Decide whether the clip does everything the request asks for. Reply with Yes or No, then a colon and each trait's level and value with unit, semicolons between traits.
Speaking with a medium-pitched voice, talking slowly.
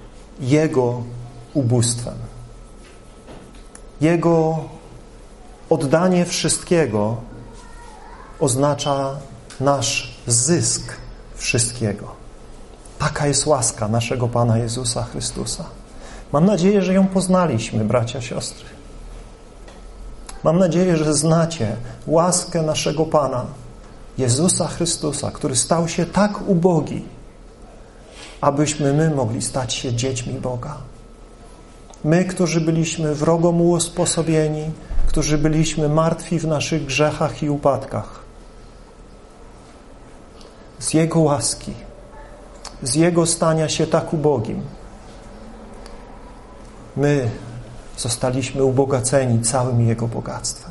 Yes: medium, 145 Hz; slow, 85 wpm